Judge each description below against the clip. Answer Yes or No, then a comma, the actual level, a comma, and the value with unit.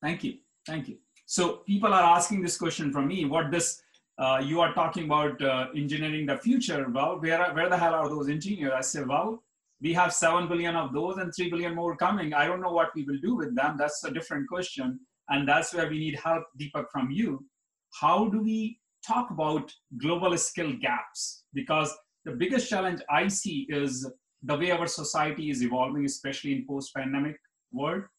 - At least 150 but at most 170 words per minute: No, average, 200 wpm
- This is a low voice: No, medium, 165 Hz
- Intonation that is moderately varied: Yes, average, 3.7 semitones